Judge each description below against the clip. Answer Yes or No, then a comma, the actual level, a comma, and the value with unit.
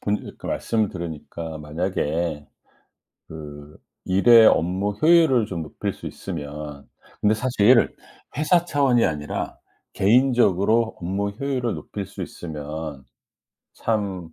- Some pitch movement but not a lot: No, wide, 6.6 semitones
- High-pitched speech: No, very low, 95 Hz